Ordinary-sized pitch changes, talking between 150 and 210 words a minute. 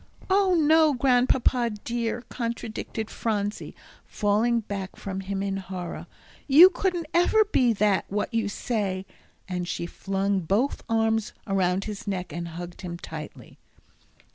No: average, 4.3 semitones; slow, 135 wpm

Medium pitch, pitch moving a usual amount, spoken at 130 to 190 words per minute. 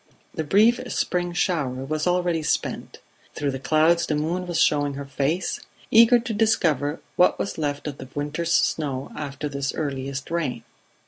Yes: medium, 155 Hz; average, 3.9 semitones; average, 165 wpm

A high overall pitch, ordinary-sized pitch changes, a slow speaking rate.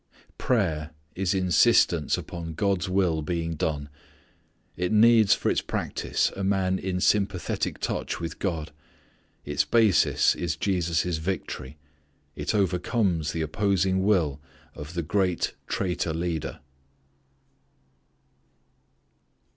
No: very low, 90 Hz; average, 3.1 semitones; slow, 105 wpm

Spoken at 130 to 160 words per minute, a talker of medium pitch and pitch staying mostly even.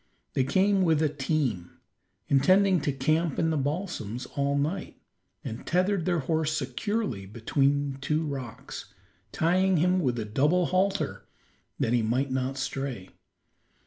No: average, 140 wpm; medium, 145 Hz; average, 5.2 semitones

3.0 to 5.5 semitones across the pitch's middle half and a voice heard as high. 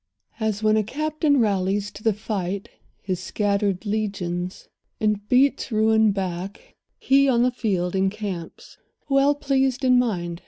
Yes: average, 4.4 semitones; high, 210 Hz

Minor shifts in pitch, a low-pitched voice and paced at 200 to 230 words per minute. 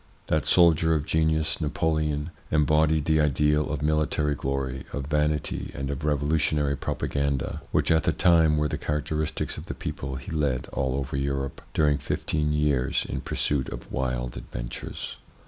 No: narrow, 2.2 semitones; very low, 75 Hz; average, 155 wpm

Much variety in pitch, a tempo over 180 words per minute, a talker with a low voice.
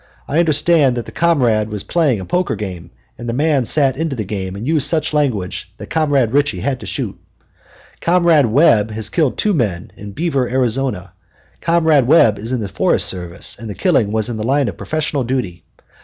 Yes: wide, 6.2 semitones; average, 200 wpm; low, 130 Hz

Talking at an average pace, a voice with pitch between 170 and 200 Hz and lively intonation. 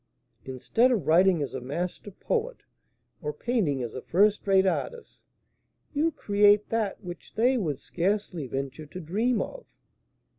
Yes: average, 145 wpm; high, 190 Hz; wide, 7.0 semitones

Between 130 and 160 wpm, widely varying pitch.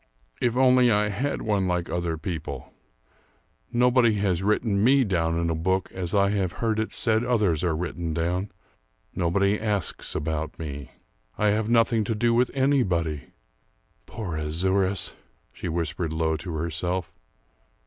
No: average, 150 wpm; average, 4.9 semitones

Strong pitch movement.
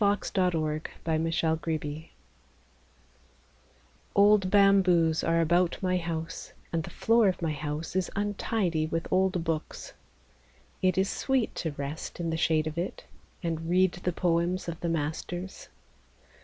No: narrow, 2.5 semitones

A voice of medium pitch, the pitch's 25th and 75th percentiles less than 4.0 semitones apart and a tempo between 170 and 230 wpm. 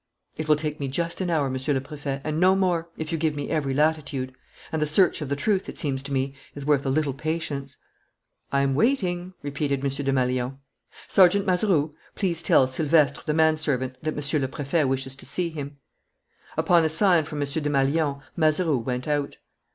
Yes: medium, 150 Hz; average, 2.7 semitones; average, 190 wpm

